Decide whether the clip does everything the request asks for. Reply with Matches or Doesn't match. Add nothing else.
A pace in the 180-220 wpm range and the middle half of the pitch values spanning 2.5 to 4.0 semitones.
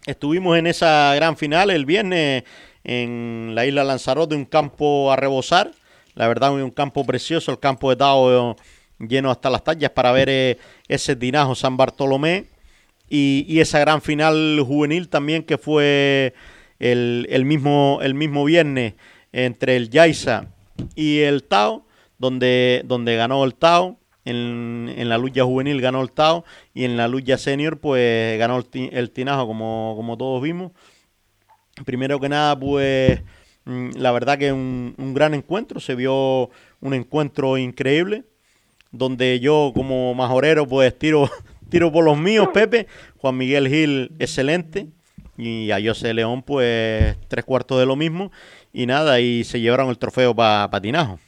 Doesn't match